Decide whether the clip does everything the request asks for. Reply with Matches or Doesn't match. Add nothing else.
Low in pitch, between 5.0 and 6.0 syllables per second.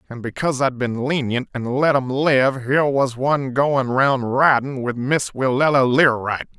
Doesn't match